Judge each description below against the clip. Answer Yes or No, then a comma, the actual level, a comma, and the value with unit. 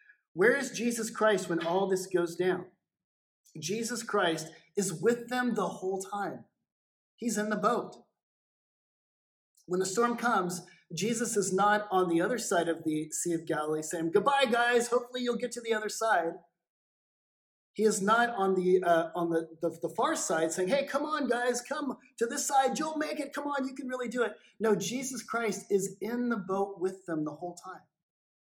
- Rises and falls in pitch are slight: No, average, 5.0 semitones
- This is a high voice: Yes, high, 210 Hz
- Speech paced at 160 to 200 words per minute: Yes, average, 190 wpm